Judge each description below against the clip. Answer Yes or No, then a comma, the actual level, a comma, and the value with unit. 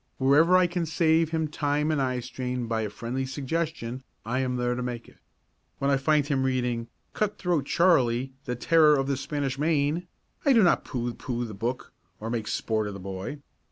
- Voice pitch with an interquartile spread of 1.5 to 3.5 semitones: No, average, 4.1 semitones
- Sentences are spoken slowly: No, average, 195 wpm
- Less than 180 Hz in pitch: Yes, low, 135 Hz